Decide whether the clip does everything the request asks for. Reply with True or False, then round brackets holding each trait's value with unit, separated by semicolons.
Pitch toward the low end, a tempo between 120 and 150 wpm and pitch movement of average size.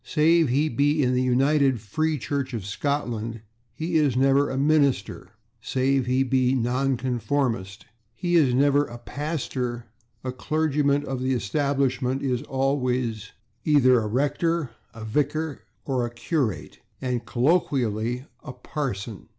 True (130 Hz; 135 wpm; 3.0 semitones)